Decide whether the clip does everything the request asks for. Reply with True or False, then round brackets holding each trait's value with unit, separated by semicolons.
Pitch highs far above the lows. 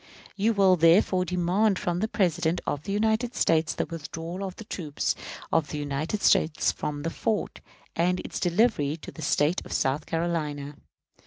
False (4.2 semitones)